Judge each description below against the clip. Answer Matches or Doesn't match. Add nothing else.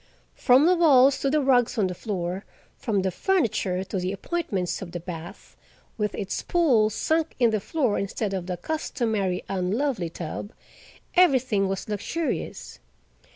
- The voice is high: Matches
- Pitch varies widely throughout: Matches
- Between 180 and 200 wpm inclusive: Doesn't match